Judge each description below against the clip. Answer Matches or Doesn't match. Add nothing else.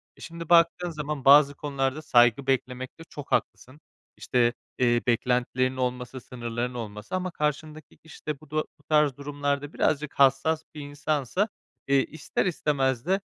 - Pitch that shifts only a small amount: Doesn't match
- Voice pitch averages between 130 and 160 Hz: Matches